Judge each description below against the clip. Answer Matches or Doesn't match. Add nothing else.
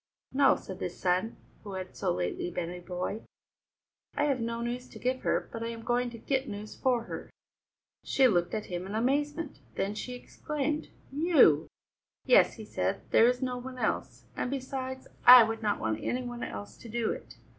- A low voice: Doesn't match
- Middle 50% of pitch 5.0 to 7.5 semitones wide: Matches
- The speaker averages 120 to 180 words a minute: Doesn't match